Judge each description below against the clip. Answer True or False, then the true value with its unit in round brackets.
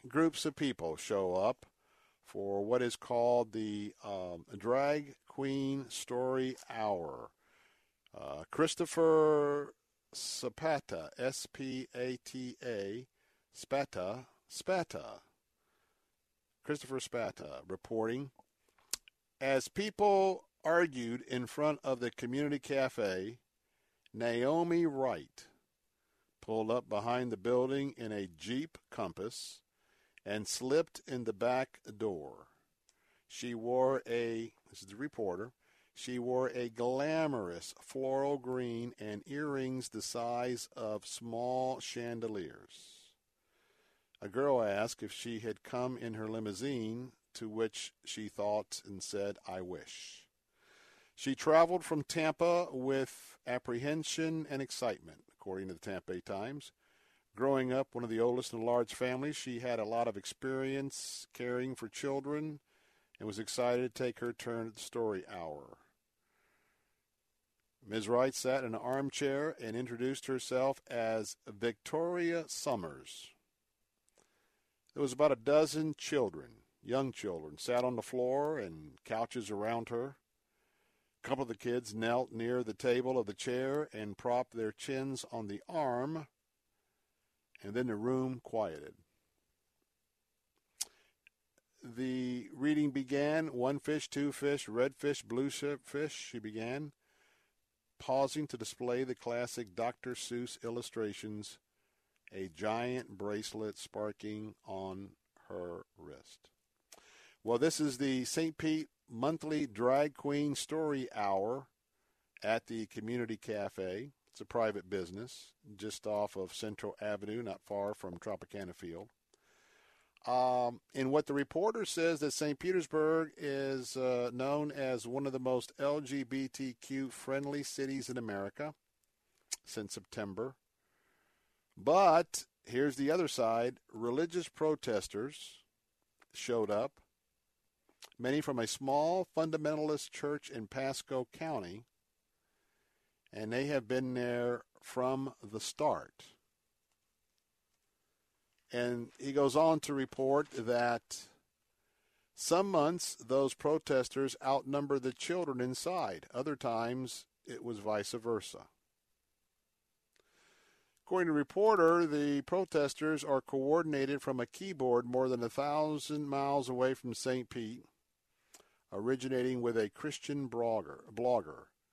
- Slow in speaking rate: True (115 wpm)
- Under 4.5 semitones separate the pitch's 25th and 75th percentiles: True (3.6 semitones)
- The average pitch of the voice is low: True (125 Hz)